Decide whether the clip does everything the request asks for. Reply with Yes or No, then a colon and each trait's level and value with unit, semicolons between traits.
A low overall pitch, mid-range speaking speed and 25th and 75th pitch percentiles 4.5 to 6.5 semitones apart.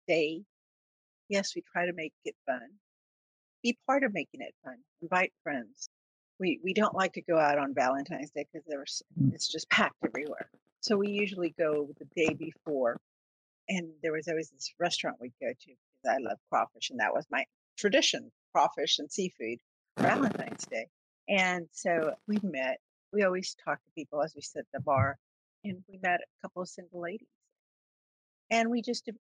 No: medium, 170 Hz; average, 180 wpm; average, 5.2 semitones